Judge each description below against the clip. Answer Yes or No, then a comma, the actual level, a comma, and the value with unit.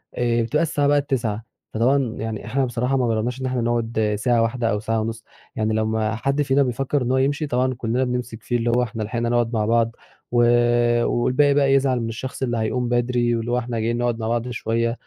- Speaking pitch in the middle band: No, low, 120 Hz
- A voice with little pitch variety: Yes, narrow, 2.2 semitones